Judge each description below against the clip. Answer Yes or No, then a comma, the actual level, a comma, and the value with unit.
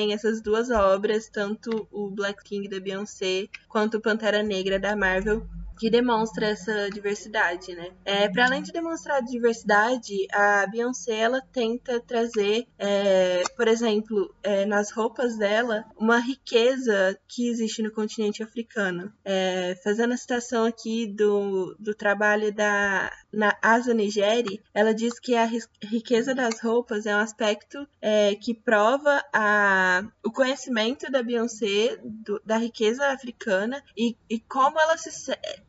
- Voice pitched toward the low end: No, high, 215 Hz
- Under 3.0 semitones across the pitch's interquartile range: Yes, narrow, 2.5 semitones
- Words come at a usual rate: Yes, average, 145 wpm